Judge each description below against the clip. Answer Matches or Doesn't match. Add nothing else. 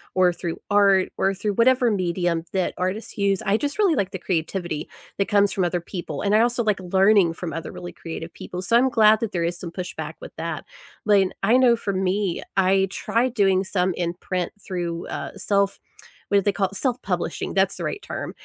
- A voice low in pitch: Doesn't match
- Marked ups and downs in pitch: Doesn't match